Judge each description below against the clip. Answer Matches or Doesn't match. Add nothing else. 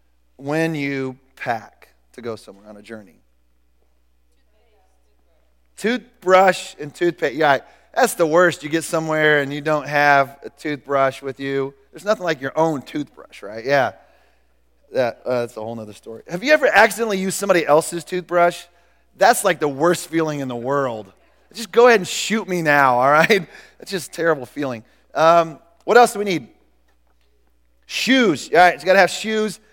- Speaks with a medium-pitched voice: Matches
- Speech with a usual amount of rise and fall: Doesn't match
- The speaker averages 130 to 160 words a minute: Doesn't match